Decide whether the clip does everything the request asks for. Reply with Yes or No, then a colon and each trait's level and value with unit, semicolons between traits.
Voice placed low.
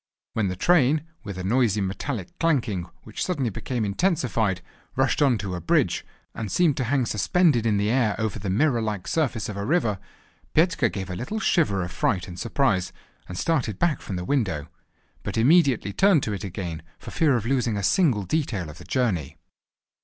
Yes: low, 115 Hz